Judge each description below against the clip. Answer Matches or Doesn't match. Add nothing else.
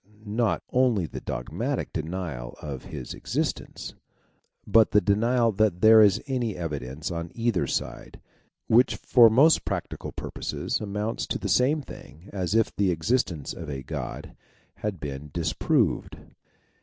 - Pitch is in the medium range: Doesn't match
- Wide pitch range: Matches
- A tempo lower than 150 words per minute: Matches